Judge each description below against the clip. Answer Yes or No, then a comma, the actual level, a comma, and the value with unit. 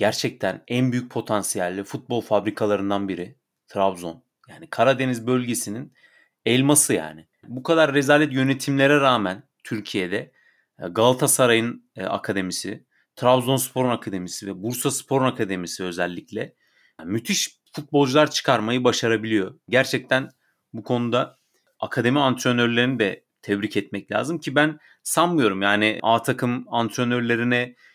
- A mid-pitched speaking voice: No, low, 120 Hz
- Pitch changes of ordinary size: Yes, average, 4.2 semitones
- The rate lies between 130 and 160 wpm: No, average, 105 wpm